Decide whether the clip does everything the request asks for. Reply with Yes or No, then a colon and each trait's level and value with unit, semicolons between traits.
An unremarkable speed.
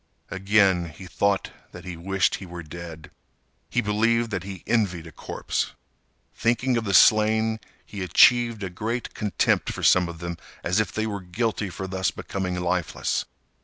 Yes: average, 165 wpm